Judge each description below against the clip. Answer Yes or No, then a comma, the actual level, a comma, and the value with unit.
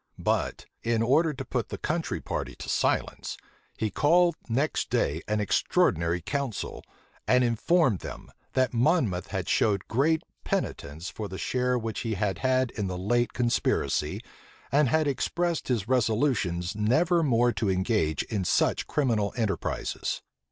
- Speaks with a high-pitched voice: No, low, 115 Hz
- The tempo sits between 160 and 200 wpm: No, average, 145 wpm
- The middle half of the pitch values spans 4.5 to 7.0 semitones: Yes, average, 5.2 semitones